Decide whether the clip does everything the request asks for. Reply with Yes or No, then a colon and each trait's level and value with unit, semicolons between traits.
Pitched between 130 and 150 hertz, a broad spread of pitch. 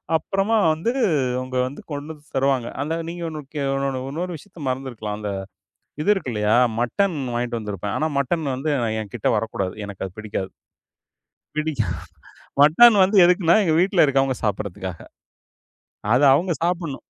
Yes: medium, 140 Hz; wide, 6.4 semitones